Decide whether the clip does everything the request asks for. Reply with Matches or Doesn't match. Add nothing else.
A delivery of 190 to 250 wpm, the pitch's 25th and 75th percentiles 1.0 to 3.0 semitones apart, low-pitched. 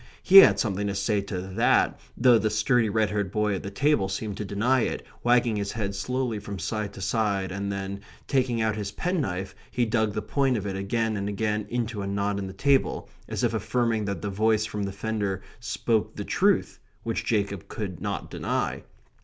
Matches